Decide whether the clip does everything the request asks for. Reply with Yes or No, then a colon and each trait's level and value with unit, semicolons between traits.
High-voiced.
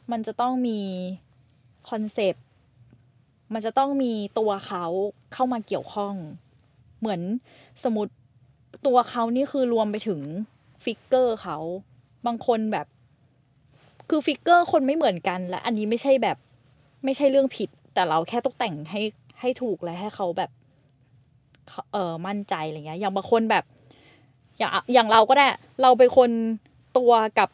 Yes: high, 205 Hz